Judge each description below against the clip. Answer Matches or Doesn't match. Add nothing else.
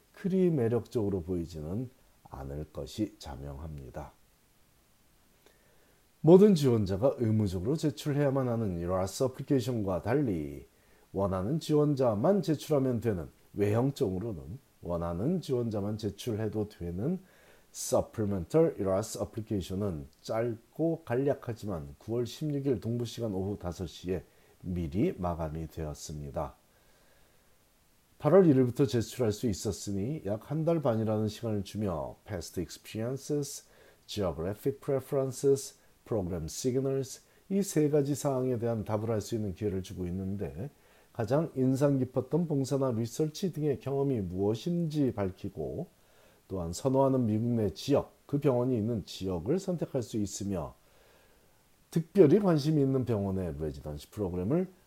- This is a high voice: Doesn't match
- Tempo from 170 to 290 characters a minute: Doesn't match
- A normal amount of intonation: Doesn't match